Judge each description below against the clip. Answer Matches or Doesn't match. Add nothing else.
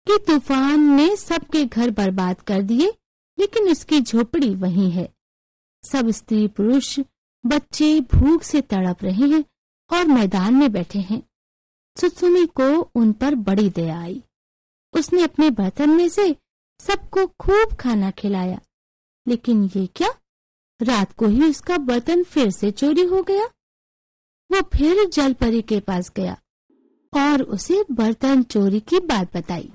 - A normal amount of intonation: Doesn't match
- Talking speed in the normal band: Matches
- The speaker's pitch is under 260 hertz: Doesn't match